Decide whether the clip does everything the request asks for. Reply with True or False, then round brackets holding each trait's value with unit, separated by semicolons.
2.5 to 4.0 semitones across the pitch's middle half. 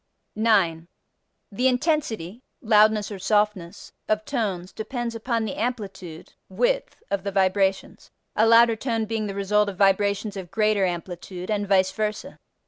True (2.8 semitones)